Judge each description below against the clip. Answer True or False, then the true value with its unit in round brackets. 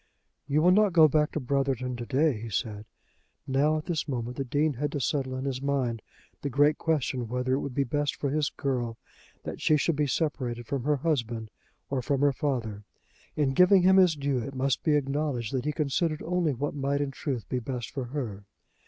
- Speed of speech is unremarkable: False (215 wpm)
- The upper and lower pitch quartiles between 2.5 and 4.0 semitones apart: True (3.2 semitones)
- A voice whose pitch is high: False (140 Hz)